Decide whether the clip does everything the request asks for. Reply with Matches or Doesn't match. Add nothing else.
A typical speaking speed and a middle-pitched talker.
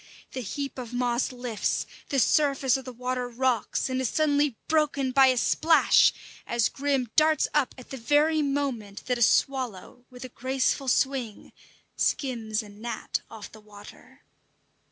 Doesn't match